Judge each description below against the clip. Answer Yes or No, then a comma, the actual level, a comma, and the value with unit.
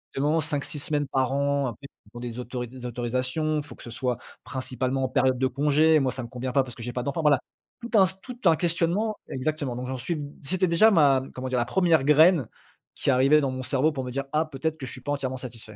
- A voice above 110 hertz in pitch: Yes, low, 135 Hz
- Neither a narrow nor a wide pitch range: Yes, average, 3.4 semitones